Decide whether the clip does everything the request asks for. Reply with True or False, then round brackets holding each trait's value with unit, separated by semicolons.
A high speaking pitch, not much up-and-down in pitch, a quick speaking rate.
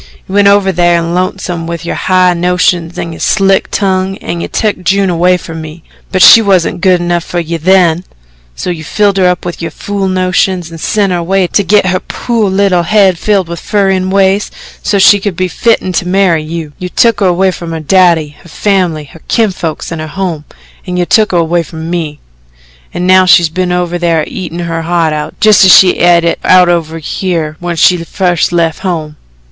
False (180 Hz; 2.2 semitones; 210 wpm)